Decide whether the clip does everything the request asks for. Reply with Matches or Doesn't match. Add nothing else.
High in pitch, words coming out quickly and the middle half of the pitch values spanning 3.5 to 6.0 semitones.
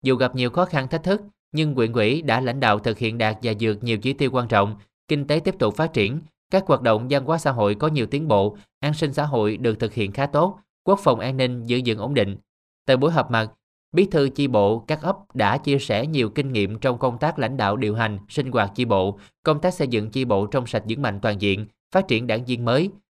Doesn't match